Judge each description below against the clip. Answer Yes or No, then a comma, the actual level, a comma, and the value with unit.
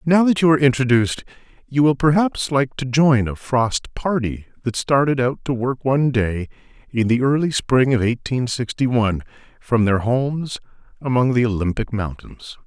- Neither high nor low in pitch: No, low, 125 Hz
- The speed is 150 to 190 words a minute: Yes, average, 170 wpm